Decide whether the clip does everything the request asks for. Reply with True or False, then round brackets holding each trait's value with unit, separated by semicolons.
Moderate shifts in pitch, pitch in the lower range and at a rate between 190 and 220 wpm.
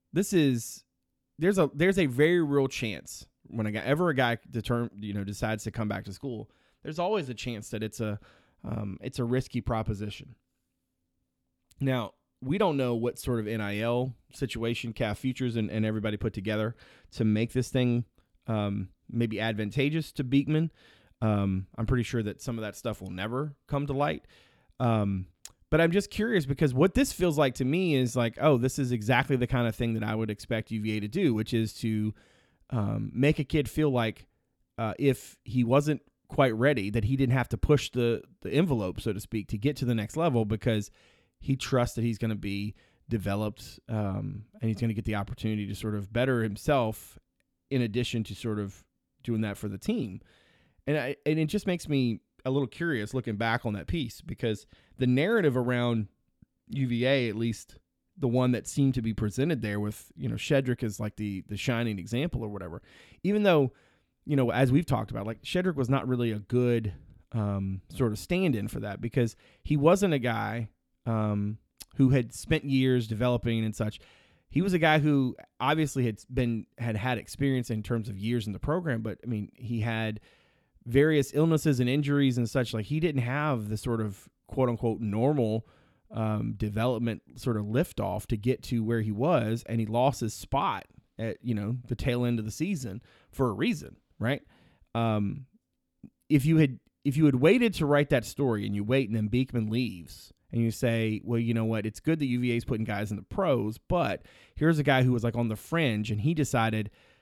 True (3.9 semitones; 120 Hz; 200 wpm)